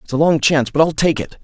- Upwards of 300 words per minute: Yes, fast, 335 wpm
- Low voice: No, medium, 150 Hz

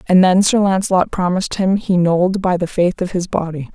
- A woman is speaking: Yes, female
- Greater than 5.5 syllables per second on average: No, 5.3 syllables/s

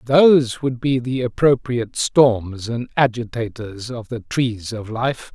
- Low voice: Yes, low, 120 Hz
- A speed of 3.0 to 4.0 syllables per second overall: Yes, 3.8 syllables/s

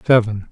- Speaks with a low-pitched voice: Yes, low, 110 Hz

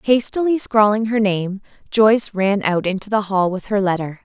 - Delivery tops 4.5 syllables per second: Yes, 5.0 syllables/s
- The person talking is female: Yes, female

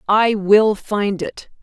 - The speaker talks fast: No, average, 150 wpm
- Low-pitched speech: No, high, 215 Hz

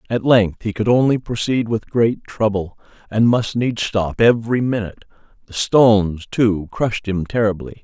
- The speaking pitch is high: No, low, 110 Hz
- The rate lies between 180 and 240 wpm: No, average, 160 wpm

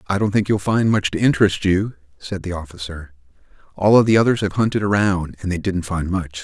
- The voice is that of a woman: No, male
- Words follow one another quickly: Yes, fast, 225 wpm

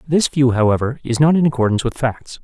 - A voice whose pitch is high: No, low, 130 Hz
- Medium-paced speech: No, fast, 220 wpm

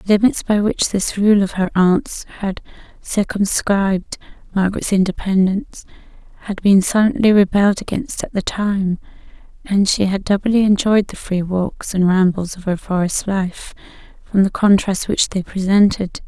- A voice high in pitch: Yes, high, 195 Hz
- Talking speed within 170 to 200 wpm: No, average, 150 wpm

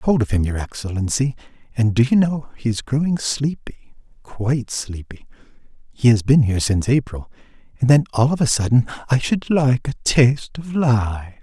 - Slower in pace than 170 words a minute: No, average, 185 wpm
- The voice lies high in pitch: No, low, 125 Hz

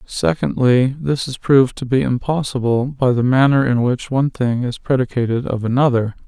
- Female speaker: No, male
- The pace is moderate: Yes, average, 170 wpm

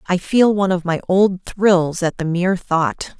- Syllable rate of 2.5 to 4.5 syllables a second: Yes, 4.4 syllables/s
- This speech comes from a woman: Yes, female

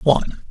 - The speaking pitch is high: No, medium, 145 Hz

